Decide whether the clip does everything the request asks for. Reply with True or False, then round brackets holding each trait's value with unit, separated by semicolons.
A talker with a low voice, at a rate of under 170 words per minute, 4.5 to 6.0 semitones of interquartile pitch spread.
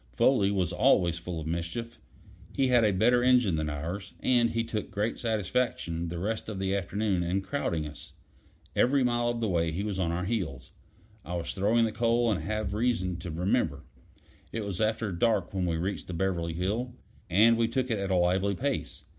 False (100 Hz; 200 wpm; 4.9 semitones)